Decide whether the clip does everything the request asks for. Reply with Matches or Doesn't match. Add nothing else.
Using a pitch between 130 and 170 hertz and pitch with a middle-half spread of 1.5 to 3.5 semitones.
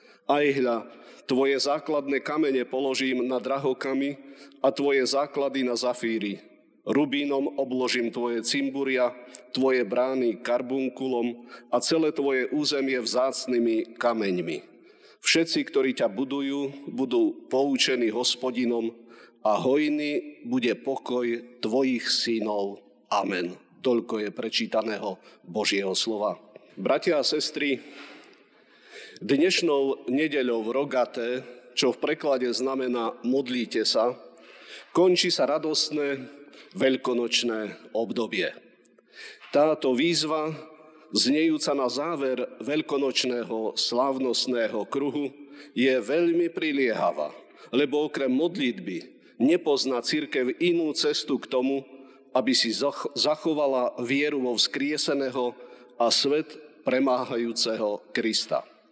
Matches